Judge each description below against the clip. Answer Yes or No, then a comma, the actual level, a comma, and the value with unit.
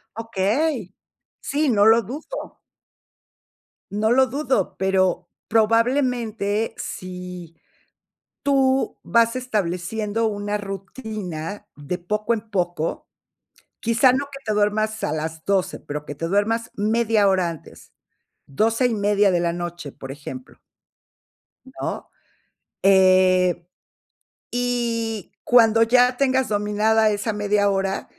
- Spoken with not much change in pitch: No, average, 3.7 semitones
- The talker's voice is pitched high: Yes, high, 210 Hz